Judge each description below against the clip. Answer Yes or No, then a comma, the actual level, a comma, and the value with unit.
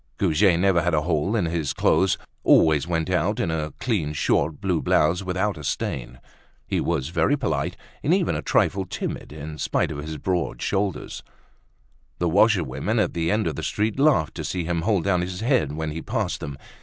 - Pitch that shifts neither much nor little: Yes, average, 4.1 semitones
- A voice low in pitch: Yes, very low, 85 Hz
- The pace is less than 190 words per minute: No, average, 195 wpm